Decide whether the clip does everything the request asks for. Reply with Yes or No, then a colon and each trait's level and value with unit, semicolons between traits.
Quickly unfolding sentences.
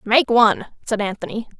No: average, 150 wpm